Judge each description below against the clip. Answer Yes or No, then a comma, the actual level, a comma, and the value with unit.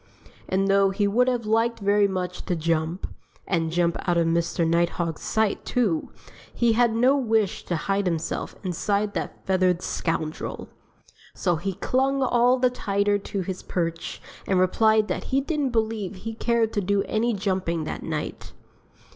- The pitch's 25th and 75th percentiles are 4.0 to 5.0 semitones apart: Yes, average, 4.4 semitones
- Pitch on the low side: No, high, 200 Hz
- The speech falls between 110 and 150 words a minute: No, average, 165 wpm